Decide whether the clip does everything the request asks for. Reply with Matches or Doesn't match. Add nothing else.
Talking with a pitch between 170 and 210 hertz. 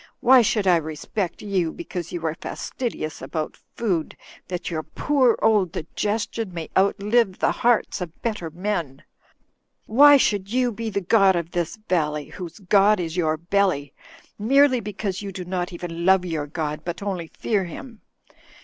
Matches